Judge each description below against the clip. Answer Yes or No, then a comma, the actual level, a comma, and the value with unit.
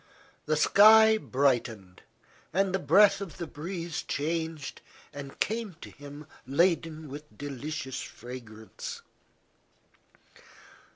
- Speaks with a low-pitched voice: No, medium, 155 Hz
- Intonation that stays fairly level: No, average, 4.8 semitones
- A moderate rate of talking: No, slow, 100 wpm